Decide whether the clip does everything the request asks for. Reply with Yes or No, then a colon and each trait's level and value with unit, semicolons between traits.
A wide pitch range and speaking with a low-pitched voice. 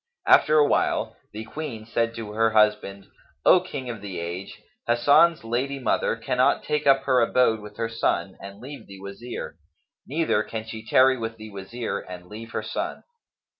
No: average, 3.8 semitones; low, 115 Hz